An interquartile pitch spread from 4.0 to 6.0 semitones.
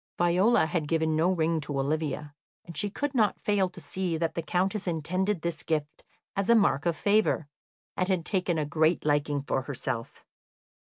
No: average, 3.6 semitones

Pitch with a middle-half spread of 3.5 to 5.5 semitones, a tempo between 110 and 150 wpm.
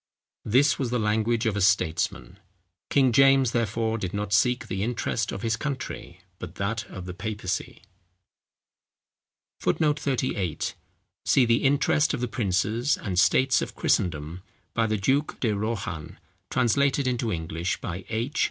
Yes: average, 4.8 semitones; average, 145 wpm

